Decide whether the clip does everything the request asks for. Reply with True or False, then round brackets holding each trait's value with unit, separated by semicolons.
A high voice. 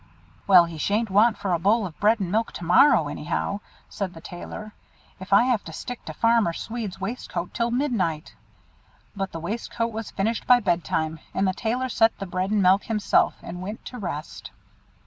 True (200 Hz)